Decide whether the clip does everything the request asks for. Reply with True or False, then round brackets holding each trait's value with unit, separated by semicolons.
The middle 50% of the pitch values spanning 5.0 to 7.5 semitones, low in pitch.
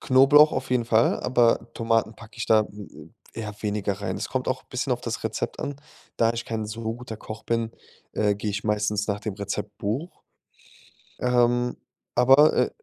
False (2.6 semitones; 115 Hz)